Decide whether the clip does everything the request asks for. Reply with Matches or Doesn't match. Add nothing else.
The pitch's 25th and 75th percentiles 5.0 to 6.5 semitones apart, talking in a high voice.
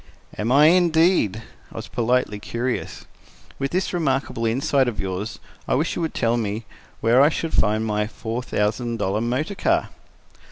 Doesn't match